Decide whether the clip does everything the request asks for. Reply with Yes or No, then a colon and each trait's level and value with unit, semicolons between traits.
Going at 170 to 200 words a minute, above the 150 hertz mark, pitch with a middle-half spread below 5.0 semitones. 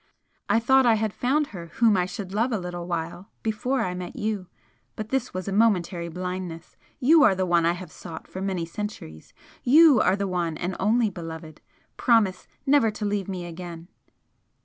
Yes: average, 190 wpm; high, 190 Hz; average, 4.2 semitones